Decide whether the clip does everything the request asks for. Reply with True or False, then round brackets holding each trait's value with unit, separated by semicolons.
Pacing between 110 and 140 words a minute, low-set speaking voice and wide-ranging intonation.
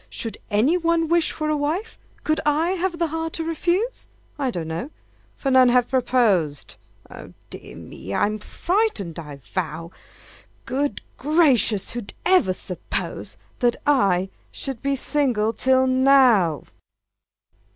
False (135 wpm; 260 Hz; 7.5 semitones)